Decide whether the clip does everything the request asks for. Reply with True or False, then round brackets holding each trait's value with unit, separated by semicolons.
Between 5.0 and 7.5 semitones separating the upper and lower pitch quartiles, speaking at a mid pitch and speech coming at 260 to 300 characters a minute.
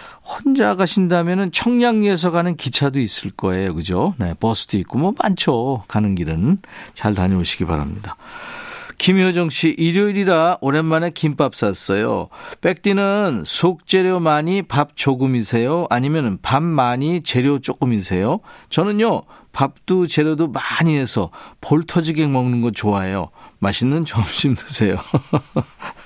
False (8.0 semitones; 155 Hz; 280 characters per minute)